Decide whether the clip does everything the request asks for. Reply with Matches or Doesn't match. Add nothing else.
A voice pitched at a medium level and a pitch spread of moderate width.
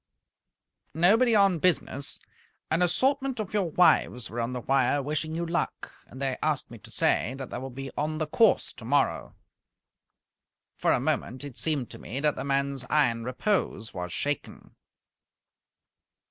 Matches